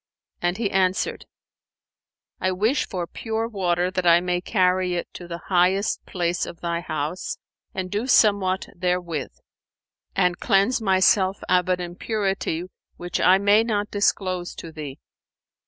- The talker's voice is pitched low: No, medium, 185 Hz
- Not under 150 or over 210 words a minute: No, average, 140 wpm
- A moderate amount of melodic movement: No, narrow, 2.1 semitones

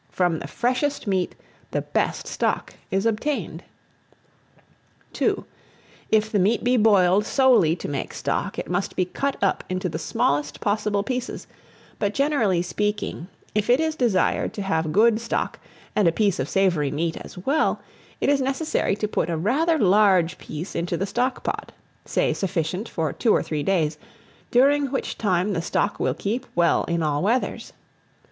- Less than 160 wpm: No, average, 165 wpm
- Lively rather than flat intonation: Yes, wide, 5.7 semitones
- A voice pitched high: Yes, high, 200 Hz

